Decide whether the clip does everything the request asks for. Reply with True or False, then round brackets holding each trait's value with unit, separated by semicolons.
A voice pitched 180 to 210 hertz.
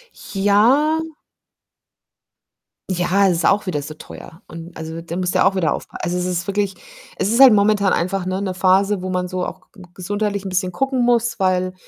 True (190 Hz)